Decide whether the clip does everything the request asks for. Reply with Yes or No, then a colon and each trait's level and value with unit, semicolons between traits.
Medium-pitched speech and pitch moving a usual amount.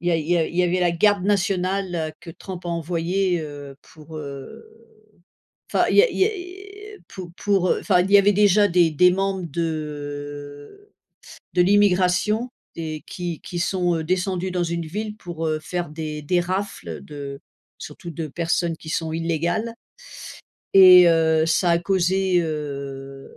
Yes: medium, 175 Hz; average, 3.2 semitones